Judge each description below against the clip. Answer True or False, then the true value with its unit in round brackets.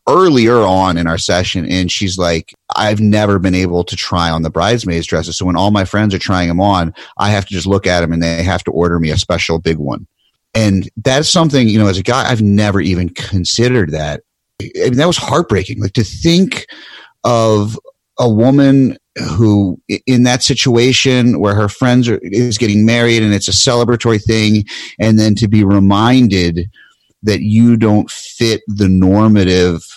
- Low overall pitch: True (105 Hz)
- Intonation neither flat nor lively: True (4.0 semitones)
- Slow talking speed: False (190 wpm)